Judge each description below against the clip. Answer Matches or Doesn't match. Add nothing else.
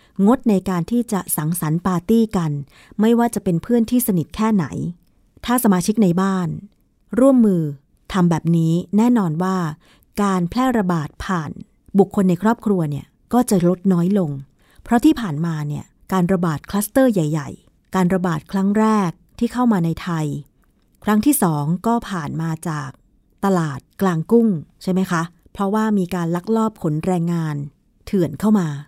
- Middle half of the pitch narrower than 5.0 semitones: Matches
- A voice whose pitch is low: Doesn't match